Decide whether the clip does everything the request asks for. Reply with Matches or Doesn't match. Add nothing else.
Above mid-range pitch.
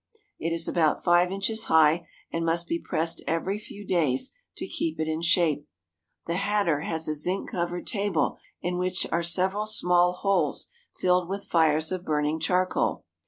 Doesn't match